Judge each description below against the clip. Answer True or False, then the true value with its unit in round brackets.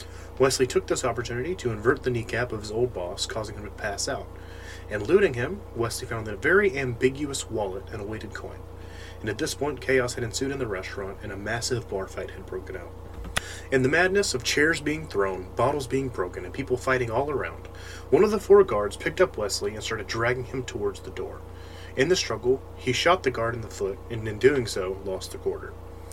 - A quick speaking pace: True (220 wpm)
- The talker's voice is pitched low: True (110 Hz)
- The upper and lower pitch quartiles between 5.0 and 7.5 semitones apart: True (5.6 semitones)